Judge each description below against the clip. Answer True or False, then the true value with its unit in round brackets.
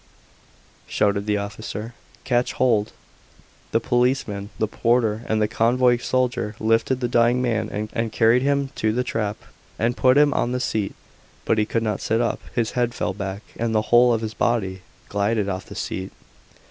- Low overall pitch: True (115 Hz)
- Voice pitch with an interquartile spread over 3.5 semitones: False (2.5 semitones)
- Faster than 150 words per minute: True (175 wpm)